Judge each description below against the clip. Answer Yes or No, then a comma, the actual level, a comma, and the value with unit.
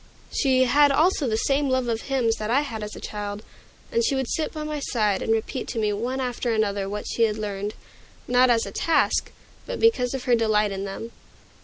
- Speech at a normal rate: No, fast, 220 wpm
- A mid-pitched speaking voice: No, high, 235 Hz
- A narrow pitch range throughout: No, average, 4.3 semitones